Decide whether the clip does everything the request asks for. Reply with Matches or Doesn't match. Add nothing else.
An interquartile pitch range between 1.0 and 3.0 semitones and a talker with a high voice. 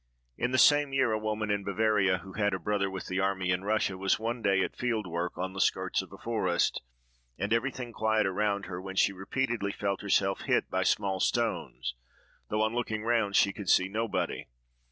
Doesn't match